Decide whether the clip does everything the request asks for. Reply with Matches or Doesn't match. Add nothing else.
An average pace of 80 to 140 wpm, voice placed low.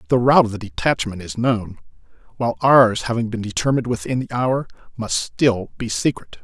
Doesn't match